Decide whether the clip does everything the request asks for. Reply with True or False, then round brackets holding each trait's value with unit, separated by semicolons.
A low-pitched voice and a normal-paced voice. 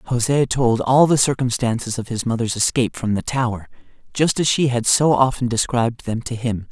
True (120 Hz; 195 wpm)